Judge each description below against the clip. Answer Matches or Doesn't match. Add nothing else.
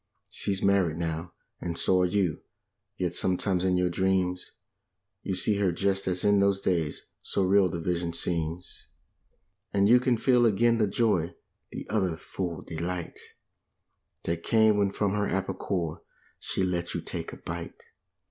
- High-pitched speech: Doesn't match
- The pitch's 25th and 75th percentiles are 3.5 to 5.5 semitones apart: Doesn't match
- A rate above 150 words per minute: Matches